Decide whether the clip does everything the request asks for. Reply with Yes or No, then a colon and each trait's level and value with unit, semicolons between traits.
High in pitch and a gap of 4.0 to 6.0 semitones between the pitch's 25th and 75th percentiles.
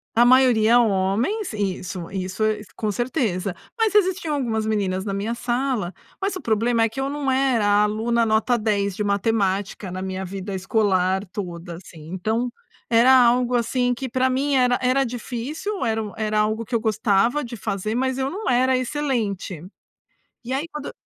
Yes: high, 225 Hz; average, 4.3 semitones